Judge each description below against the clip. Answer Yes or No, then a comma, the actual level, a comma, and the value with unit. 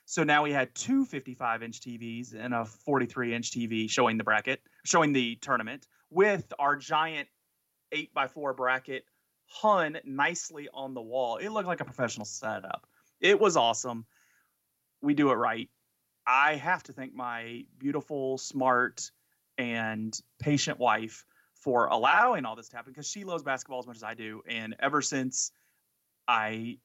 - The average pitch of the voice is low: Yes, low, 130 Hz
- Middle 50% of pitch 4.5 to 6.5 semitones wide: No, average, 3.9 semitones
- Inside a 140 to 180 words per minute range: Yes, average, 165 wpm